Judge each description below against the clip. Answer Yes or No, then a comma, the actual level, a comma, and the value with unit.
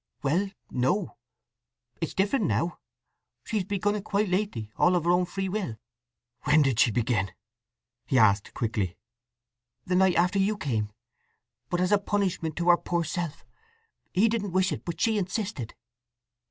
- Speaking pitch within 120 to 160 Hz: No, medium, 175 Hz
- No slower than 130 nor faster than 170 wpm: Yes, average, 150 wpm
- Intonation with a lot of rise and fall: Yes, wide, 8.1 semitones